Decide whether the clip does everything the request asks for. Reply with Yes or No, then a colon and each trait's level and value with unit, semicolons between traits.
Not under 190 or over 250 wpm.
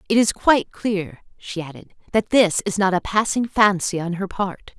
Yes: average, 200 wpm